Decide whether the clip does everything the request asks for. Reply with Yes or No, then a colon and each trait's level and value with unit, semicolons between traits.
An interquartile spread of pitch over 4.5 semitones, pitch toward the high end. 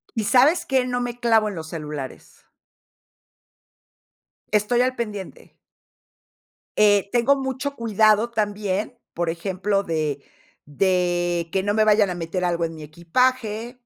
Yes: average, 5.3 semitones; high, 205 Hz